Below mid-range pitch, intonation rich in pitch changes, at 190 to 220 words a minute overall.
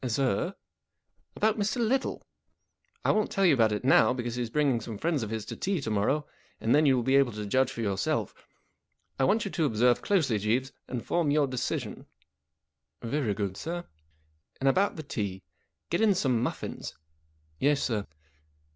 Yes: low, 130 Hz; wide, 6.2 semitones; average, 200 wpm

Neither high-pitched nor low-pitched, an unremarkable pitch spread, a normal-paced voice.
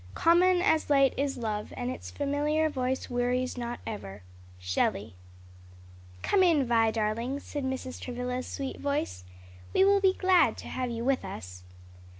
No: very high, 255 Hz; average, 4.3 semitones; average, 150 wpm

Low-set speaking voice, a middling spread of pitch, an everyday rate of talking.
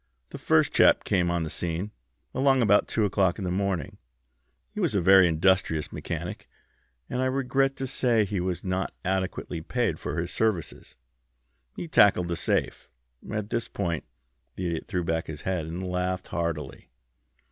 Yes: very low, 95 Hz; average, 3.6 semitones; average, 170 wpm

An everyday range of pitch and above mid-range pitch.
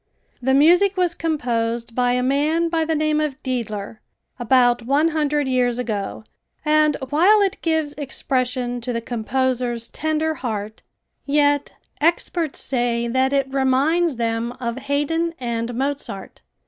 Yes: average, 4.1 semitones; very high, 265 Hz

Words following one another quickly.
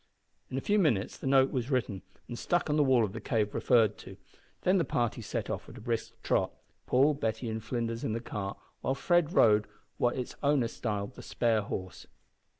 Yes: fast, 210 wpm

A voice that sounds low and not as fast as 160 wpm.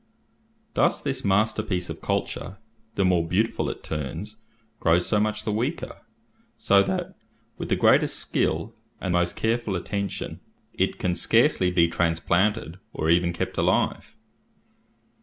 Yes: very low, 95 Hz; slow, 135 wpm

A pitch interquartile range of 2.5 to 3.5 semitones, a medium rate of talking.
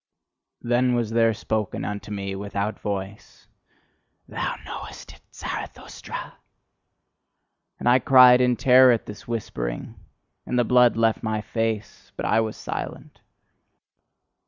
No: average, 2.8 semitones; slow, 125 wpm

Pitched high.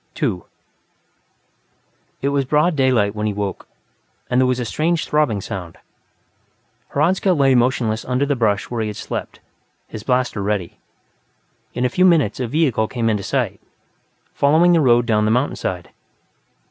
No: low, 125 Hz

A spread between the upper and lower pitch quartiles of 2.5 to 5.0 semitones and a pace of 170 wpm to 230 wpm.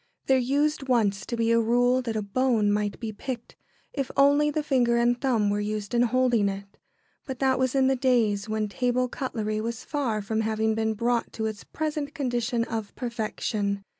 Yes: average, 3.2 semitones; average, 195 wpm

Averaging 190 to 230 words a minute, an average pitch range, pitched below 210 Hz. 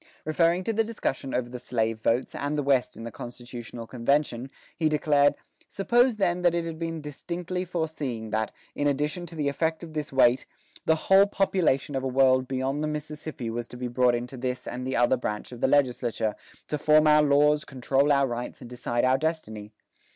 Yes: average, 200 wpm; average, 4.2 semitones; medium, 140 Hz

